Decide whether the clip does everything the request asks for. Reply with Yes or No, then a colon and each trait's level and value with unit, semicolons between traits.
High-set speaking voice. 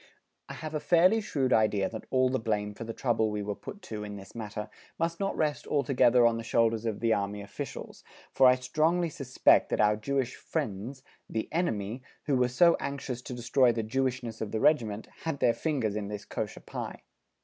No: low, 120 Hz